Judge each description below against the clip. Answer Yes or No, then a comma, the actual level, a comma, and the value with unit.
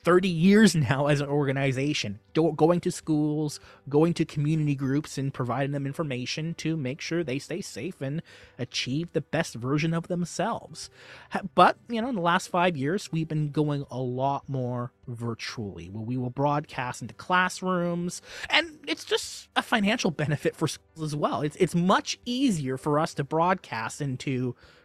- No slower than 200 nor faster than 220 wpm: No, average, 170 wpm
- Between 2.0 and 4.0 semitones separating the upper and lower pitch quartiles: No, average, 4.5 semitones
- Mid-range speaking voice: Yes, medium, 150 Hz